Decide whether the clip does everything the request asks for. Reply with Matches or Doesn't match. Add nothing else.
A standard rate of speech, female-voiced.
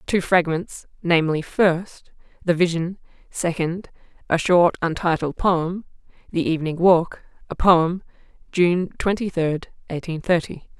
Doesn't match